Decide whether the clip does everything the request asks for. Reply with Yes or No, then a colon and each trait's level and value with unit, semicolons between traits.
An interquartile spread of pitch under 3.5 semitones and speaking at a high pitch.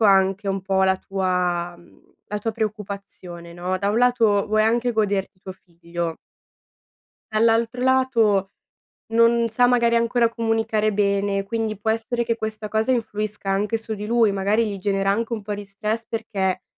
Yes: average, 2.7 semitones; high, 210 Hz